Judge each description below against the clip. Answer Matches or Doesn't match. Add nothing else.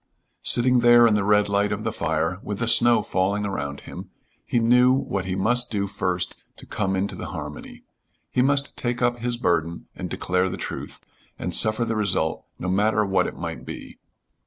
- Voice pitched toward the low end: Matches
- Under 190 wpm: Doesn't match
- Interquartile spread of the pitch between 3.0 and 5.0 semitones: Matches